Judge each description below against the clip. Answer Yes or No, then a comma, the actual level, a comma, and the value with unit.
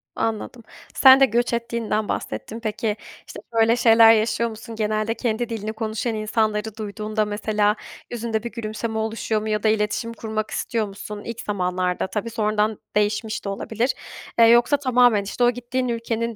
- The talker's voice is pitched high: Yes, high, 220 Hz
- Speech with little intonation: Yes, narrow, 1.6 semitones